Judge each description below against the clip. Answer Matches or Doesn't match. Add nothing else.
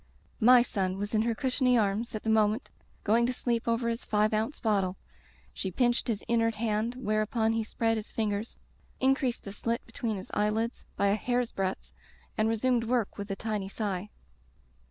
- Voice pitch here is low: Doesn't match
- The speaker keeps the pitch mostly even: Matches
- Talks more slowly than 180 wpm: Doesn't match